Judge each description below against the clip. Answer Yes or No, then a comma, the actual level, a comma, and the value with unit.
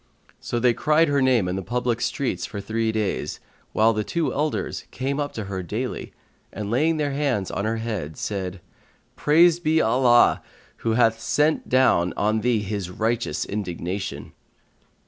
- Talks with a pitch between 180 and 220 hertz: No, low, 115 Hz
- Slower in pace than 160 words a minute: No, average, 165 wpm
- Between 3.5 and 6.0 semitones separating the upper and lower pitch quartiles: Yes, average, 5.2 semitones